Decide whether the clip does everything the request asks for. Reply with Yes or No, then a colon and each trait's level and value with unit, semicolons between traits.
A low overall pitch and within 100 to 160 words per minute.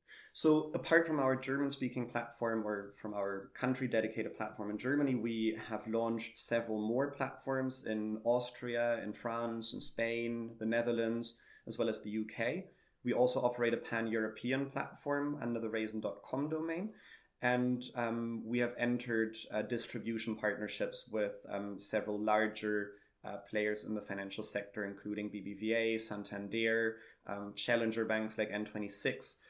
Yes: low, 115 Hz; average, 140 wpm